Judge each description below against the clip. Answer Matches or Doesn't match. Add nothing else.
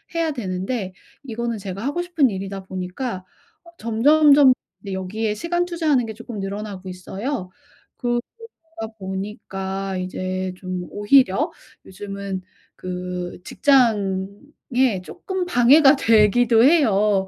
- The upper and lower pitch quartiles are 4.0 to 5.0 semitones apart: Doesn't match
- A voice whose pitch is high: Matches